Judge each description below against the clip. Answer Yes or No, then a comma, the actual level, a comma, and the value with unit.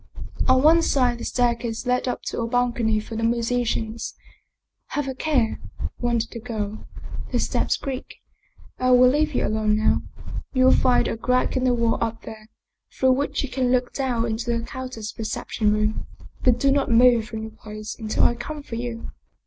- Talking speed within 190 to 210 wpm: Yes, average, 195 wpm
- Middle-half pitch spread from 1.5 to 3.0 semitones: Yes, narrow, 2.4 semitones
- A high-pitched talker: Yes, high, 240 Hz